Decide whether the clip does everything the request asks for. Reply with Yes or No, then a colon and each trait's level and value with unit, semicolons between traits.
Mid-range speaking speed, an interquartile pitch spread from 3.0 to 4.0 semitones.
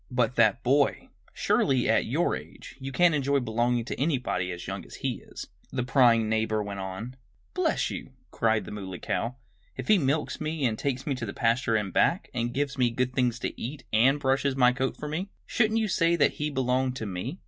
No: fast, 215 wpm; average, 3.6 semitones